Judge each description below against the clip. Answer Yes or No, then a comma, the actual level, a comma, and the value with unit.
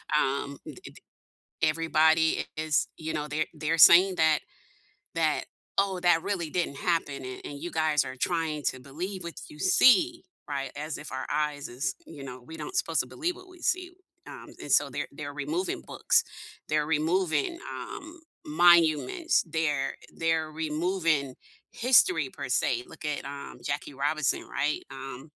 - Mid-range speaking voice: Yes, medium, 155 Hz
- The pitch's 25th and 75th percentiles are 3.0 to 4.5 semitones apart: Yes, average, 3.6 semitones